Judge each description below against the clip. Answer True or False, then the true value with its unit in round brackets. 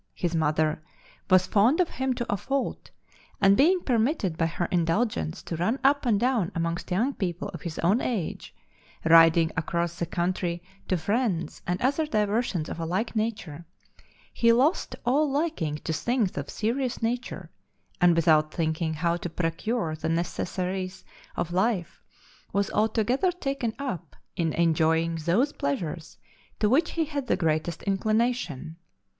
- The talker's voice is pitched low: False (185 Hz)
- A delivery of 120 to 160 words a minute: True (155 wpm)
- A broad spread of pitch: True (6.4 semitones)